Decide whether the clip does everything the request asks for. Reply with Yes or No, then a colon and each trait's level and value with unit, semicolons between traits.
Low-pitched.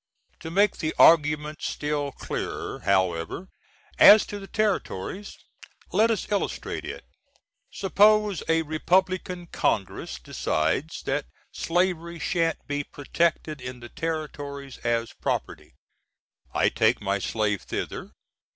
No: medium, 160 Hz